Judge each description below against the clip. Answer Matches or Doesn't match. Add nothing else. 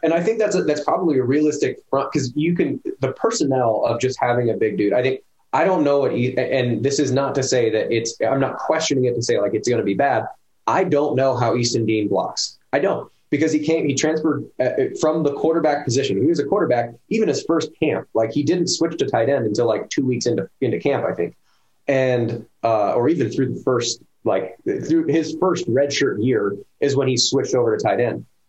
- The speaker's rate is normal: Doesn't match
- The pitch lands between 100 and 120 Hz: Doesn't match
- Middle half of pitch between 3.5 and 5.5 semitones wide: Matches